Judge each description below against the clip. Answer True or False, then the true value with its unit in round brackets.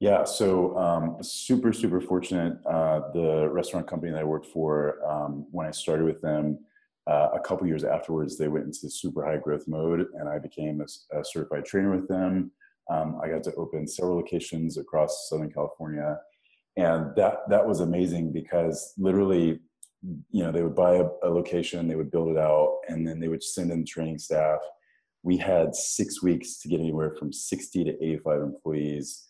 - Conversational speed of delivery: True (190 wpm)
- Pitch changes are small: True (2.3 semitones)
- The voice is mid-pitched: False (80 Hz)